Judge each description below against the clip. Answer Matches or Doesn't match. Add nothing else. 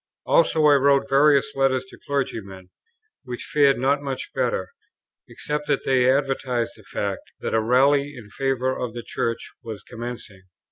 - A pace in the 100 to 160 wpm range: Matches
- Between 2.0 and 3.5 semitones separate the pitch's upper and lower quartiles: Matches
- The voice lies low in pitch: Matches